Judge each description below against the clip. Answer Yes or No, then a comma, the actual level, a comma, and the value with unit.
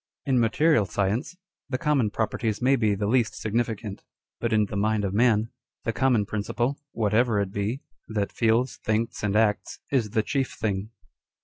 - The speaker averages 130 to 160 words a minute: No, average, 170 wpm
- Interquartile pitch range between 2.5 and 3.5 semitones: Yes, average, 2.8 semitones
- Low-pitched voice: Yes, low, 110 Hz